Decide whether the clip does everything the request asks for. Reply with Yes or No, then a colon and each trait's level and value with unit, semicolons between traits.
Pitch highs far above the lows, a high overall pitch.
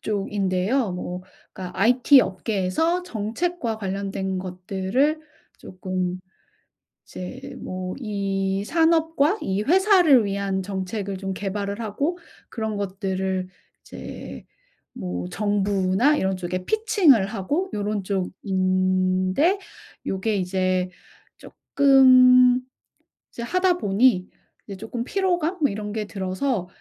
Yes: wide, 5.8 semitones; high, 200 Hz